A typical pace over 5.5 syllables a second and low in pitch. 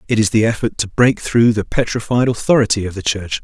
Yes: 5.9 syllables/s; low, 110 Hz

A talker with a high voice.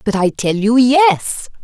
Yes: high, 215 Hz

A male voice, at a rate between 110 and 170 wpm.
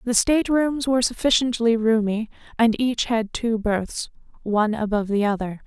No: female; average, 160 wpm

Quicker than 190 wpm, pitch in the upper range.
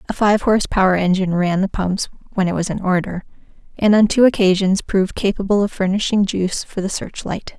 Yes: fast, 205 wpm; high, 195 Hz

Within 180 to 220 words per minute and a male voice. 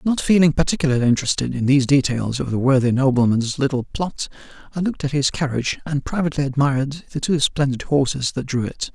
Yes: average, 190 wpm; male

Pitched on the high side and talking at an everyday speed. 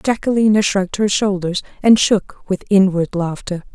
Yes: high, 195 Hz; average, 145 wpm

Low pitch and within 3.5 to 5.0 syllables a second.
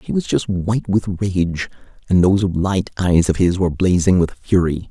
Yes: very low, 90 Hz; 4.8 syllables/s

